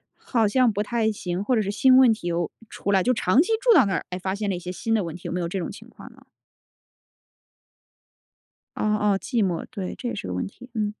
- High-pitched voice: Yes, high, 205 Hz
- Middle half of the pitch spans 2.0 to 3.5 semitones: No, average, 4.3 semitones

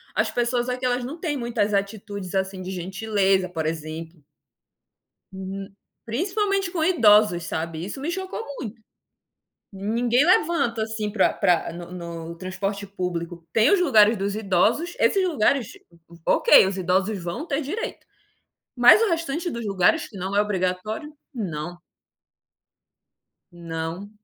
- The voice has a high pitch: Yes, high, 205 Hz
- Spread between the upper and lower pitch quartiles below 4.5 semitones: No, wide, 5.6 semitones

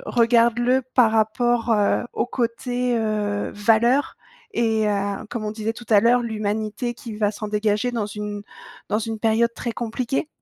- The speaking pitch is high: Yes, high, 225 Hz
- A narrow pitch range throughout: Yes, narrow, 2.2 semitones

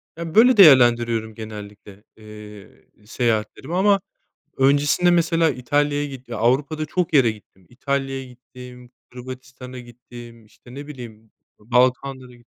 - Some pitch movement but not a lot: Yes, average, 3.7 semitones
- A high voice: No, low, 125 Hz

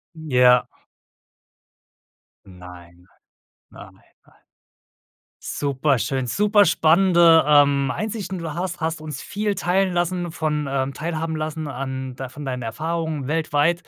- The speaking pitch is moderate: Yes, medium, 155 Hz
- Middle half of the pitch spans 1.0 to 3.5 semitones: No, average, 4.6 semitones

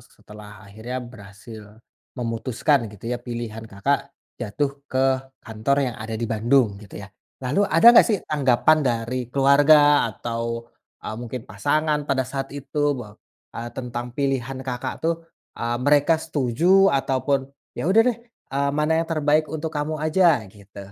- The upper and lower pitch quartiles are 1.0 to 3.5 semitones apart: No, average, 4.2 semitones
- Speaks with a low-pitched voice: Yes, low, 130 Hz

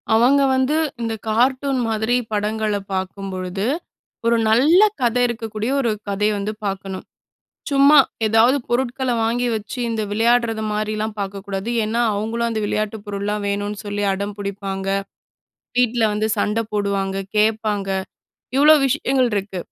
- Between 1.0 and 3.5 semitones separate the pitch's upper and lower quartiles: Yes, average, 2.9 semitones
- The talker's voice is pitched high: Yes, high, 215 Hz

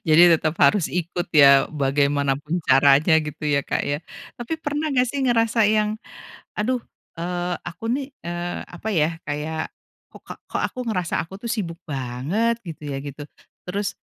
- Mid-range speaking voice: Yes, medium, 175 Hz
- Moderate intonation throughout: No, wide, 6.7 semitones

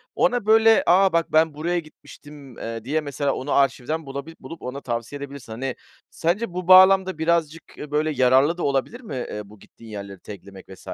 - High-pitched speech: No, medium, 145 Hz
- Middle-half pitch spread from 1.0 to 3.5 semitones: No, average, 4.9 semitones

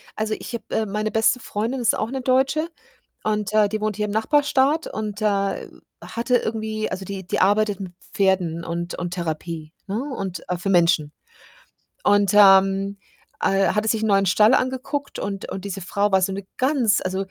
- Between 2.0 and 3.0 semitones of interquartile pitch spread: Yes, narrow, 2.5 semitones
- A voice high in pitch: Yes, high, 205 Hz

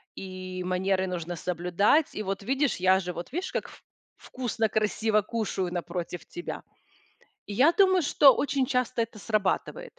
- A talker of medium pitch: No, high, 210 Hz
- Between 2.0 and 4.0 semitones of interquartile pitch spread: No, wide, 5.6 semitones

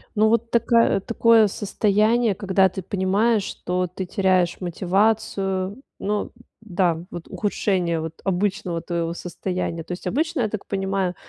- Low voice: No, high, 195 Hz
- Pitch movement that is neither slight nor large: Yes, average, 3.1 semitones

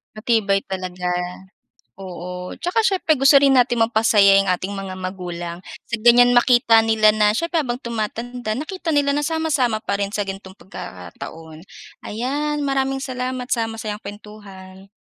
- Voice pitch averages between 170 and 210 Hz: No, high, 220 Hz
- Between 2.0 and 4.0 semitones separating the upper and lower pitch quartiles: No, average, 4.9 semitones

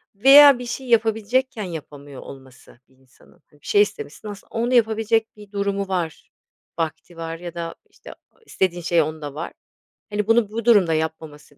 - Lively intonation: Yes, wide, 5.8 semitones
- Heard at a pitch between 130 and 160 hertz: No, high, 195 Hz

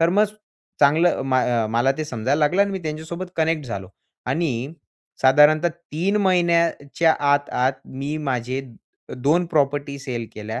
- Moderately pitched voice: Yes, medium, 150 Hz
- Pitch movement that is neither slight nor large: Yes, average, 4.1 semitones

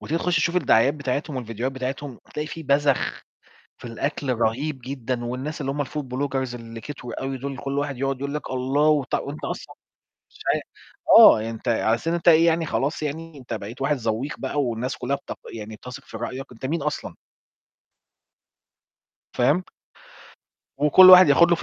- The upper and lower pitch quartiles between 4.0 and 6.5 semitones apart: No, average, 3.3 semitones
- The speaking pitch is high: No, low, 135 Hz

